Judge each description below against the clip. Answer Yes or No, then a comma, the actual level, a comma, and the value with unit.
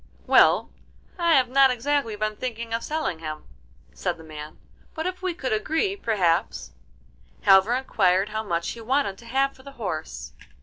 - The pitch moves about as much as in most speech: No, wide, 6.3 semitones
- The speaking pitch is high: Yes, high, 230 Hz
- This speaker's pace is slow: No, average, 170 wpm